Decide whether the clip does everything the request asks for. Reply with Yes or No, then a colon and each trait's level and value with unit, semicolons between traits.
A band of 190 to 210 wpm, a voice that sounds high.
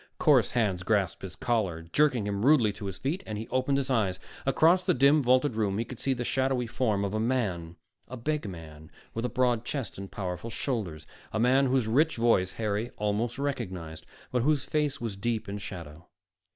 No: average, 200 wpm; low, 115 Hz